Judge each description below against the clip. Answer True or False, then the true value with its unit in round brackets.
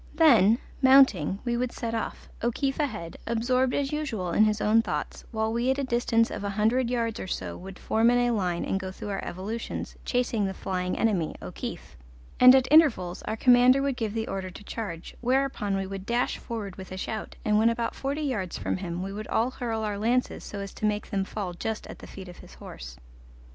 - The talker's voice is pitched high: True (220 Hz)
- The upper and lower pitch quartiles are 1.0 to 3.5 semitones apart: False (4.1 semitones)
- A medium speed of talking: False (215 wpm)